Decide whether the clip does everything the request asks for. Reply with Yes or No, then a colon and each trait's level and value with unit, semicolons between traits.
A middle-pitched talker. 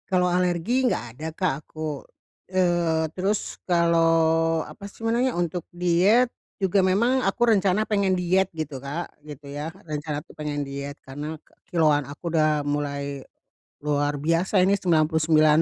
Yes: medium, 165 Hz